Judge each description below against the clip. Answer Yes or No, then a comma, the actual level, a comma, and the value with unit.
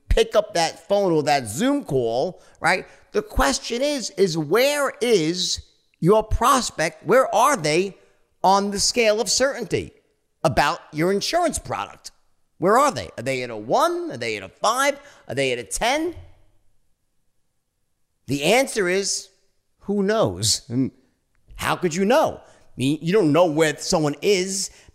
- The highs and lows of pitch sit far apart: Yes, wide, 7.8 semitones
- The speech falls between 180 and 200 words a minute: No, average, 155 wpm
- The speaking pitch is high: No, medium, 180 Hz